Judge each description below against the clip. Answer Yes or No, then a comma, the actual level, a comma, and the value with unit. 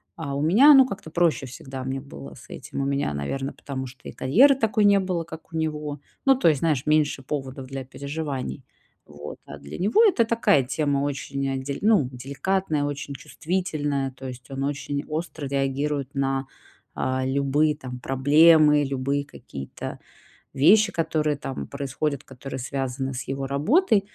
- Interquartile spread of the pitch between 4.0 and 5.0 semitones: No, average, 3.1 semitones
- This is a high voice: No, medium, 140 Hz